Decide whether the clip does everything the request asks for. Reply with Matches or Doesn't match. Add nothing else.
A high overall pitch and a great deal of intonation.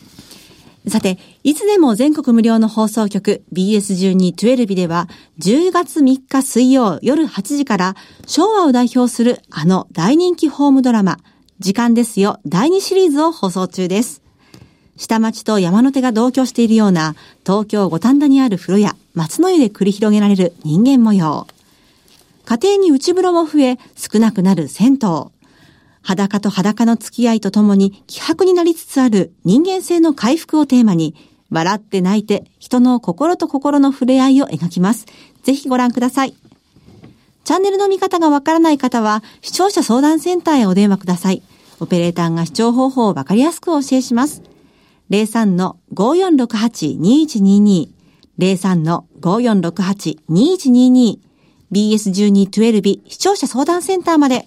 Matches